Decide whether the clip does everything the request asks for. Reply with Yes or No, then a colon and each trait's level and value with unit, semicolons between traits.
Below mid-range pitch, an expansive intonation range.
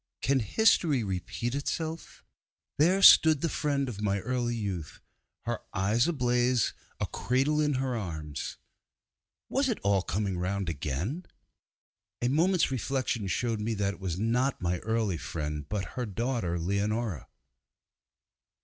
Yes: low, 115 Hz; wide, 5.9 semitones